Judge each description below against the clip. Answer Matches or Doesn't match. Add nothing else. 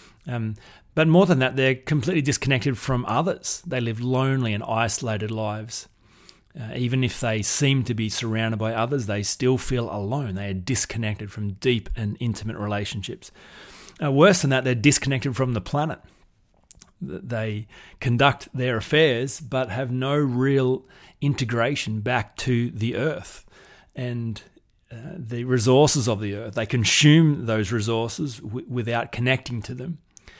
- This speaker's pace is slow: Doesn't match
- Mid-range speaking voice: Doesn't match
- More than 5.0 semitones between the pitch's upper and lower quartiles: Doesn't match